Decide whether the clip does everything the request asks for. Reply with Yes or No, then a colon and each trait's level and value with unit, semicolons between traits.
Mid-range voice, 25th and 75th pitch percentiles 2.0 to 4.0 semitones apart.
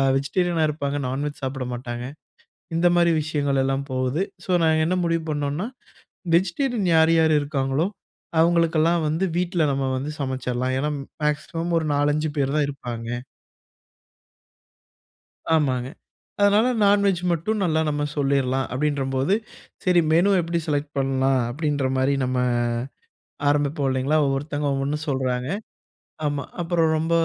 Yes: medium, 145 Hz; average, 3.6 semitones